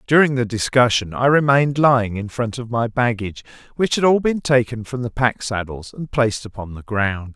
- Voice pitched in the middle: No, low, 120 Hz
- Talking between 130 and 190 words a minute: No, fast, 205 wpm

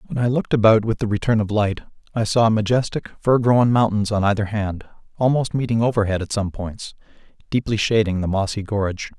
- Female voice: No, male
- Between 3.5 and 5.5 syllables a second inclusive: No, 5.7 syllables/s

